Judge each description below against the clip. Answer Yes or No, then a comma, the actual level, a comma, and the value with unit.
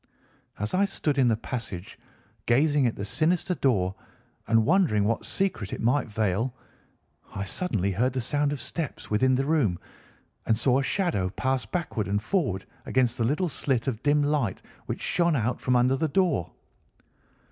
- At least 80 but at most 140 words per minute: No, average, 170 wpm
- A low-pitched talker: Yes, low, 130 Hz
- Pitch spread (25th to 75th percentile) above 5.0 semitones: Yes, wide, 5.4 semitones